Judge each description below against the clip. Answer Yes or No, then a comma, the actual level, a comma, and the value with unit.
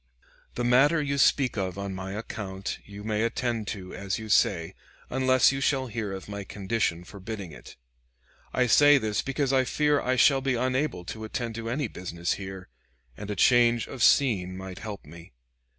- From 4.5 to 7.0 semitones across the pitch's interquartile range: Yes, average, 5.1 semitones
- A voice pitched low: Yes, low, 110 Hz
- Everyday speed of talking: Yes, average, 185 wpm